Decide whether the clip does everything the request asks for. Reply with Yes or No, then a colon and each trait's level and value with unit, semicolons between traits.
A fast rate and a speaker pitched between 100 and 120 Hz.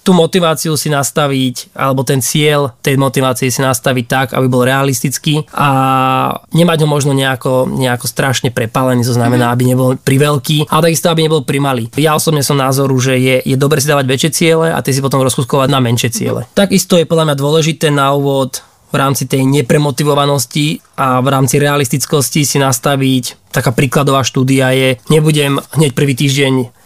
No: fast, 175 wpm; medium, 140 Hz